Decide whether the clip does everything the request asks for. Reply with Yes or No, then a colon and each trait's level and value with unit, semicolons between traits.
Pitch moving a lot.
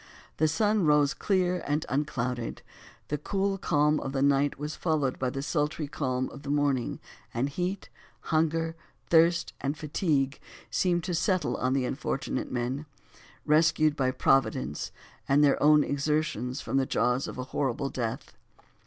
No: average, 2.9 semitones